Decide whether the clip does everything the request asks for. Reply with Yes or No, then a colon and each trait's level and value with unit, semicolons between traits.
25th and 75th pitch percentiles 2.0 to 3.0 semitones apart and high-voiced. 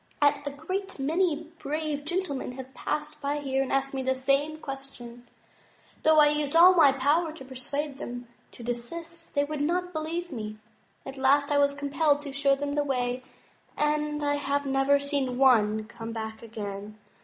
Yes: narrow, 2.4 semitones; very high, 280 Hz